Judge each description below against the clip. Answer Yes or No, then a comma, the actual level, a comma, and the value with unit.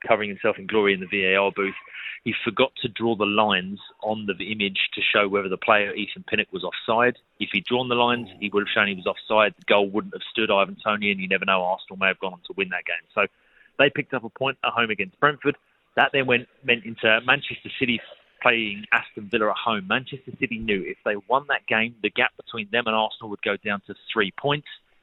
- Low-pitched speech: Yes, low, 110 Hz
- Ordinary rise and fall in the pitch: Yes, average, 3.7 semitones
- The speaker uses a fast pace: Yes, fast, 235 wpm